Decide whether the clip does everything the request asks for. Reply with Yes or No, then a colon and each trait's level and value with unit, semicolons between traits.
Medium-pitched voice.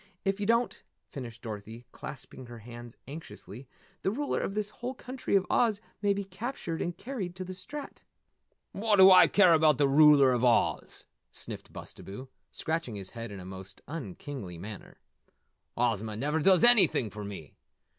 Yes: medium, 150 Hz